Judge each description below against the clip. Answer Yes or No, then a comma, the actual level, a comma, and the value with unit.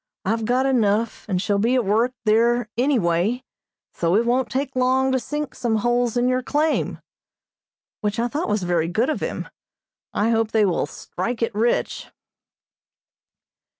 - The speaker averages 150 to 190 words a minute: Yes, average, 165 wpm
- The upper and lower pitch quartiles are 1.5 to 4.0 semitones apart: Yes, average, 3.3 semitones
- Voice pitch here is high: Yes, high, 235 Hz